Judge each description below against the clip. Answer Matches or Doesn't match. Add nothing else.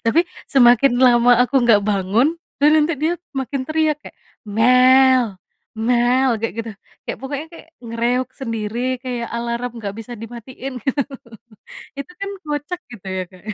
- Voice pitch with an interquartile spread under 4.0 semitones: Matches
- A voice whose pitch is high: Matches